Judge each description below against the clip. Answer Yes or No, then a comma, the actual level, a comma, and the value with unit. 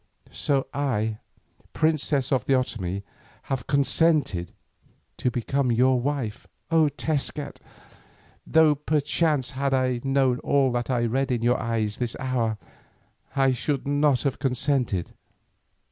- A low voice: Yes, low, 130 Hz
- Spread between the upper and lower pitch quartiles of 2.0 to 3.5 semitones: Yes, average, 2.9 semitones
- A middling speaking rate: No, slow, 125 wpm